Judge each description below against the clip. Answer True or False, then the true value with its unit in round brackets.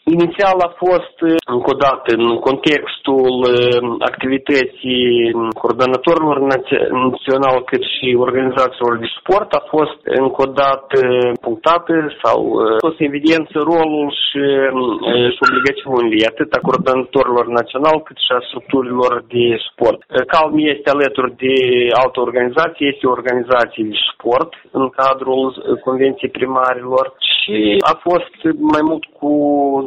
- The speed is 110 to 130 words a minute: True (115 wpm)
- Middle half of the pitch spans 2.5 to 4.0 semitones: True (3.1 semitones)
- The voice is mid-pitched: False (130 Hz)